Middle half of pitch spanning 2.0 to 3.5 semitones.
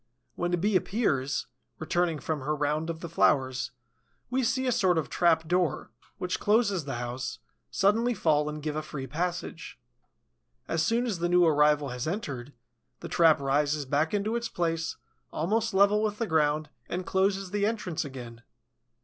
No: average, 5.0 semitones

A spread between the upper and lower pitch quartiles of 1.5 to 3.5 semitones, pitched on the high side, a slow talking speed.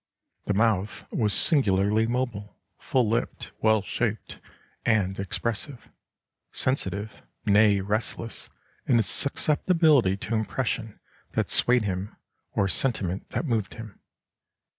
No: average, 3.2 semitones; low, 110 Hz; slow, 110 wpm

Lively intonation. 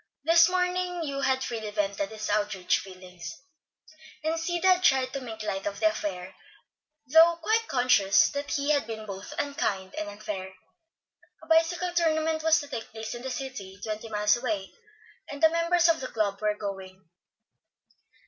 Yes: wide, 7.8 semitones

